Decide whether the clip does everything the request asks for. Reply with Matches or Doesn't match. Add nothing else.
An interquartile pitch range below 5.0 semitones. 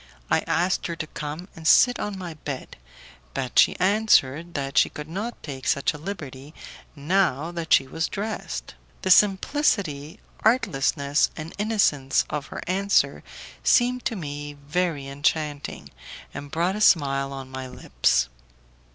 Doesn't match